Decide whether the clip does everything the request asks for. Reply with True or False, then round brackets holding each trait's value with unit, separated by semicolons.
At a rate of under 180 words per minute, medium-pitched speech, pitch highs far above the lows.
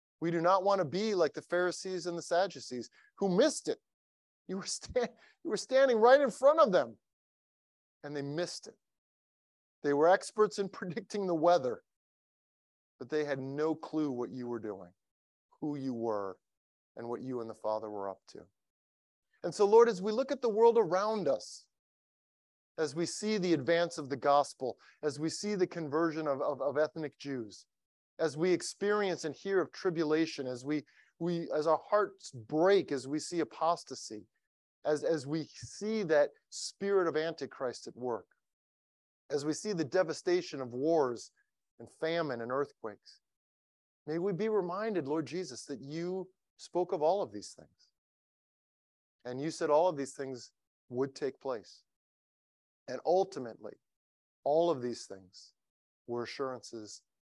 True (165 wpm; 160 Hz; 6.3 semitones)